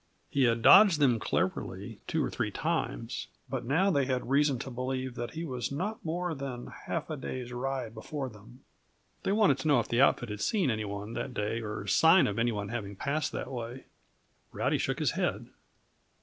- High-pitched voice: No, low, 130 Hz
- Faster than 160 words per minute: Yes, average, 200 wpm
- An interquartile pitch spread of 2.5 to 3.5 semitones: No, average, 4.1 semitones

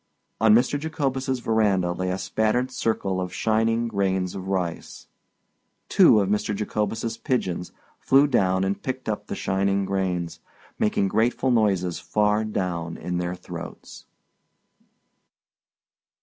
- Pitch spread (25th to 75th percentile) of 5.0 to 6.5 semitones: No, average, 3.4 semitones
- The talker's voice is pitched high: No, low, 105 Hz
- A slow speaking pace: Yes, slow, 125 wpm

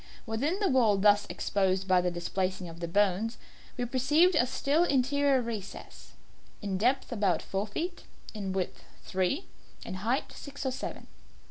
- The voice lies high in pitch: Yes, high, 220 Hz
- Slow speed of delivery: No, average, 155 wpm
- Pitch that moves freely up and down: Yes, wide, 6.0 semitones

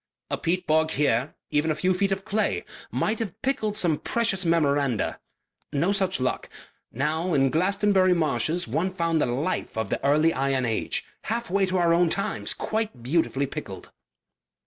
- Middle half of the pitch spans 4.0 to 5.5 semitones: Yes, average, 5.2 semitones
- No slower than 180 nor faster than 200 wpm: No, average, 170 wpm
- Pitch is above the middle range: No, medium, 165 Hz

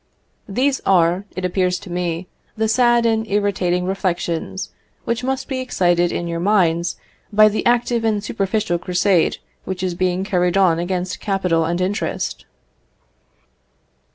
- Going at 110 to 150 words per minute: Yes, average, 140 wpm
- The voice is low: No, high, 190 Hz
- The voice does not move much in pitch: No, average, 3.4 semitones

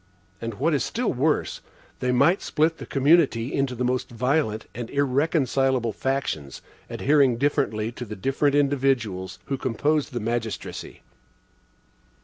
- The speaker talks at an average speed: No, slow, 130 wpm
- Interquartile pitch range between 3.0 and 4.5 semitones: Yes, average, 3.7 semitones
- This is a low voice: Yes, low, 130 Hz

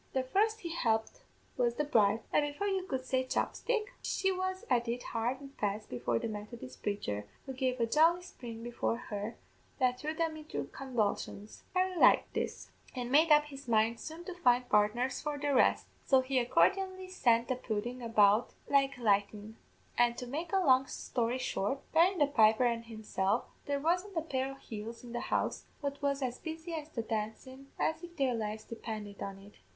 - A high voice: Yes, very high, 255 Hz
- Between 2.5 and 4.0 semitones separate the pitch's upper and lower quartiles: No, average, 5.1 semitones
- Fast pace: No, average, 190 wpm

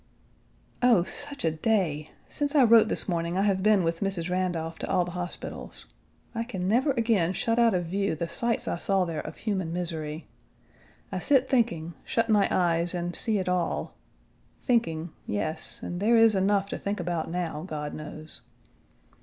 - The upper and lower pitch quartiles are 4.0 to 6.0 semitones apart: Yes, average, 4.9 semitones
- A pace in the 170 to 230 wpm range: Yes, average, 180 wpm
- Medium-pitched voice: Yes, medium, 180 Hz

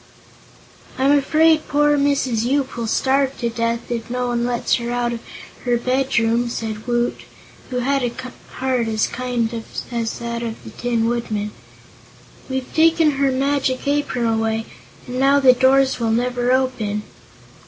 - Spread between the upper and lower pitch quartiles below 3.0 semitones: Yes, narrow, 2.5 semitones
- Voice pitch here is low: No, high, 245 Hz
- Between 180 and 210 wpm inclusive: No, average, 155 wpm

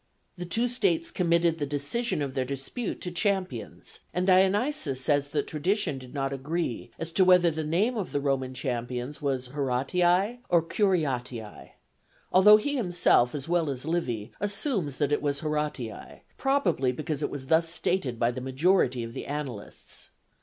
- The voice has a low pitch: No, medium, 150 Hz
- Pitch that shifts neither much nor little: No, wide, 5.7 semitones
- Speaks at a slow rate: No, average, 165 wpm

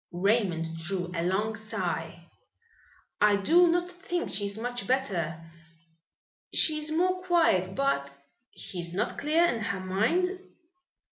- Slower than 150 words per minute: Yes, average, 140 wpm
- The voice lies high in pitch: Yes, high, 220 Hz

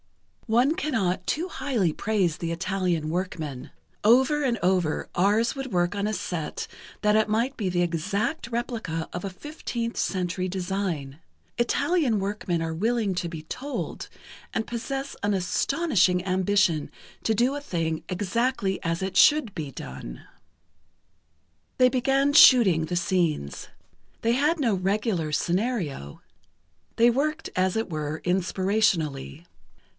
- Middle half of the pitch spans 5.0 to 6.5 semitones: Yes, wide, 5.6 semitones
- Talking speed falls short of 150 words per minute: Yes, slow, 135 wpm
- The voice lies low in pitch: No, high, 195 Hz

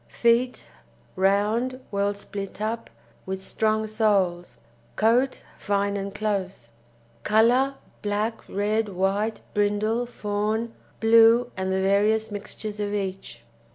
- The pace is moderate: No, slow, 110 wpm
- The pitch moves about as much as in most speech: No, narrow, 2.0 semitones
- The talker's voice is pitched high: Yes, high, 210 Hz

